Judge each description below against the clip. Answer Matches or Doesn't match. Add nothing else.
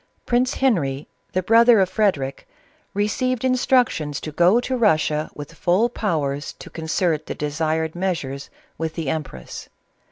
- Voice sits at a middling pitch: Matches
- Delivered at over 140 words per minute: Doesn't match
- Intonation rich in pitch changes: Matches